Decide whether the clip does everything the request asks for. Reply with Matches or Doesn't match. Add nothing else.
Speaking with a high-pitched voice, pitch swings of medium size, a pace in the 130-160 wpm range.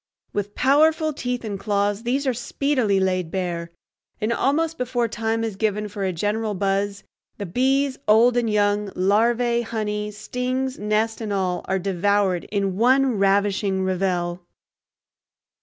Matches